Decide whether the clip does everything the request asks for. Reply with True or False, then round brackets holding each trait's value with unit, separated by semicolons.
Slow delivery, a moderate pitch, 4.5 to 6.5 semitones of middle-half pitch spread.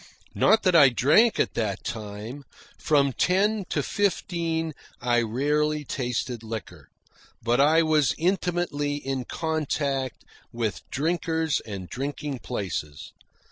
True (115 wpm; 145 Hz; 5.2 semitones)